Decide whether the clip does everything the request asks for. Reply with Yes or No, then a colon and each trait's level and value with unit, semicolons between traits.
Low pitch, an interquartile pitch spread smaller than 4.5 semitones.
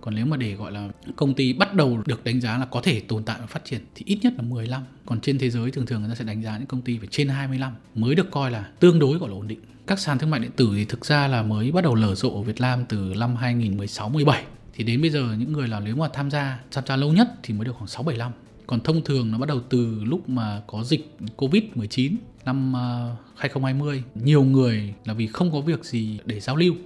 Yes: low, 125 Hz; average, 4.0 semitones